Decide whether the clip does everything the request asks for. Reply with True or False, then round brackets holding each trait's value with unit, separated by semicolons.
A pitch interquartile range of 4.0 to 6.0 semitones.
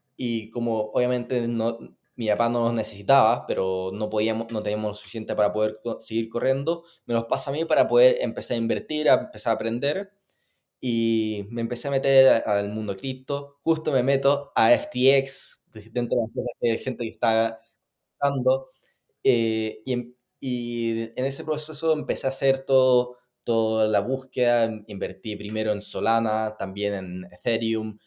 False (3.4 semitones)